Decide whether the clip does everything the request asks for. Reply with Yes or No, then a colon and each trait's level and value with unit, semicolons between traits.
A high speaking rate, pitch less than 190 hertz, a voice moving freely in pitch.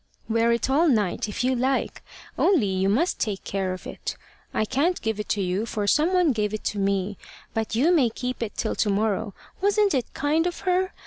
No: fast, 210 wpm; high, 230 Hz; wide, 6.5 semitones